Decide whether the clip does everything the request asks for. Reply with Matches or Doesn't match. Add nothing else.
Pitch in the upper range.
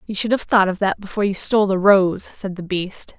Matches